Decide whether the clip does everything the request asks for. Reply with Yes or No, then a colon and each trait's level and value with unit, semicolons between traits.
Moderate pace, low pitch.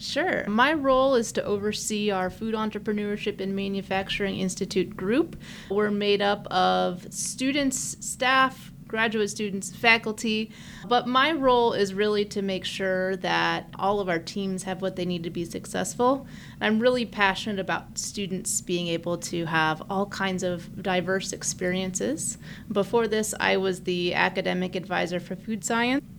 No: average, 150 wpm; high, 195 Hz